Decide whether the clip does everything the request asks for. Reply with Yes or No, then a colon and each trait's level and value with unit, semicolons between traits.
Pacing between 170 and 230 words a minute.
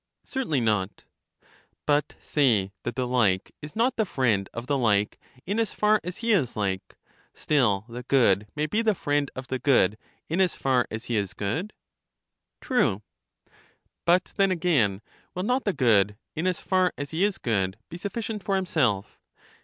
Yes: average, 175 wpm